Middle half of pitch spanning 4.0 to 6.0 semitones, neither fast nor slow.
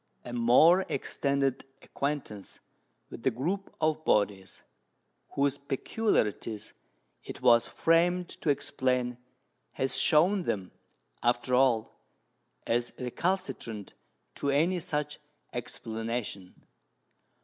No: average, 4.9 semitones; slow, 95 wpm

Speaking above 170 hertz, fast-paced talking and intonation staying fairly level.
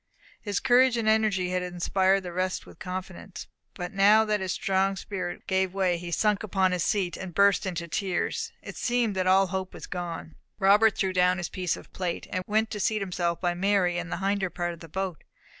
Yes: high, 190 Hz; fast, 215 wpm; narrow, 2.0 semitones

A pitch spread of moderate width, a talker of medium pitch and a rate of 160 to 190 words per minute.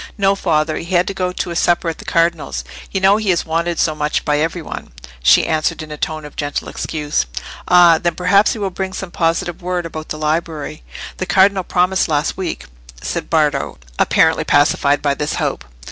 No: average, 3.0 semitones; medium, 165 Hz; fast, 205 wpm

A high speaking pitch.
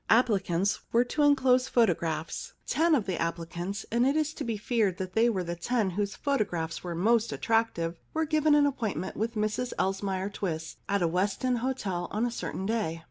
Yes: high, 210 Hz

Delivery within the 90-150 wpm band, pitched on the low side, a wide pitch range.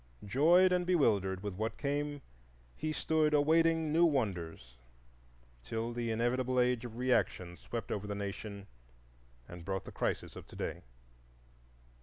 Yes: average, 140 wpm; low, 120 Hz; wide, 6.7 semitones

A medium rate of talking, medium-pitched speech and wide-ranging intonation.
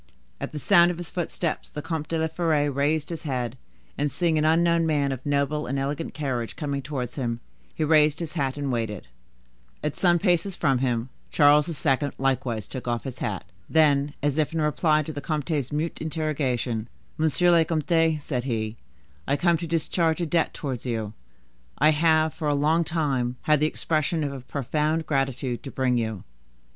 No: average, 190 wpm; medium, 150 Hz; average, 3.2 semitones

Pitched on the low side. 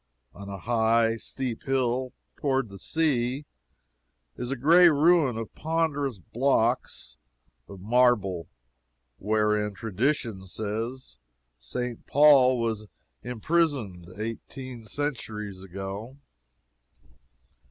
Yes: low, 120 Hz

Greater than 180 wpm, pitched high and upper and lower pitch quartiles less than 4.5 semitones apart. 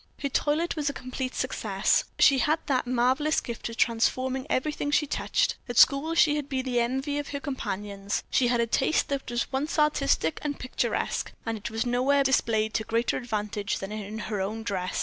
Yes: average, 200 wpm; very high, 255 Hz; average, 4.1 semitones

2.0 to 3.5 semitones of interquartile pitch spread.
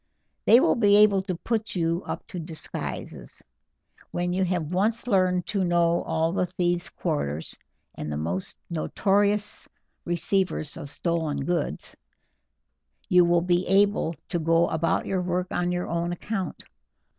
Yes: narrow, 2.5 semitones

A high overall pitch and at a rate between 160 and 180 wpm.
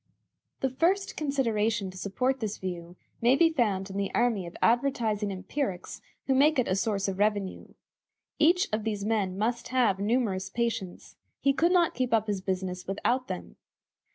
Yes: high, 220 Hz; average, 170 wpm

